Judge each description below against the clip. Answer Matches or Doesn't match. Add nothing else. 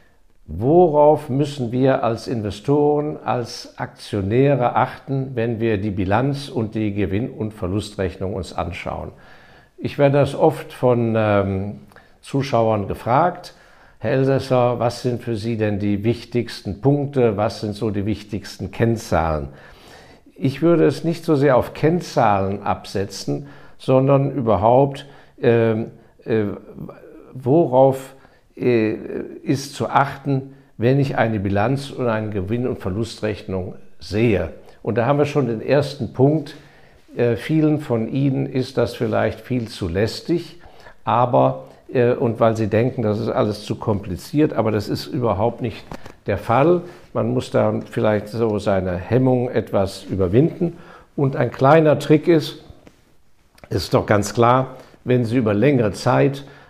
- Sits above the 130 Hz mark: Doesn't match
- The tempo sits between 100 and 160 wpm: Matches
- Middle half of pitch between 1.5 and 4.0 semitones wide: Doesn't match